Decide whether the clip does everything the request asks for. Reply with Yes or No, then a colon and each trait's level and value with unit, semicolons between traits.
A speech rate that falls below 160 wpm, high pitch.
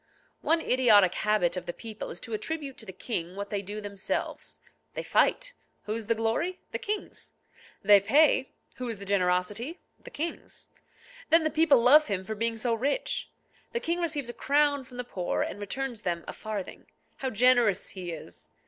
No: average, 180 wpm; high, 230 Hz